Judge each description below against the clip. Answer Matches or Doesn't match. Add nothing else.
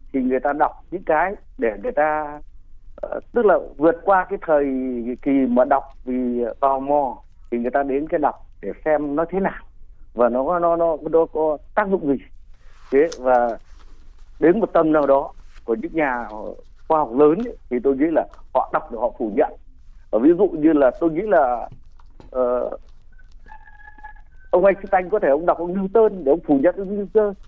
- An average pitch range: Doesn't match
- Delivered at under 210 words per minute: Matches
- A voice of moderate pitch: Matches